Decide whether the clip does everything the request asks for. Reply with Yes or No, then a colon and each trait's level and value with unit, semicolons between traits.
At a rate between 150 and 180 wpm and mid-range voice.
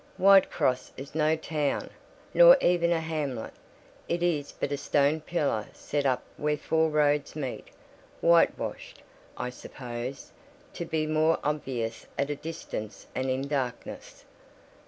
No: slow, 135 wpm; medium, 150 Hz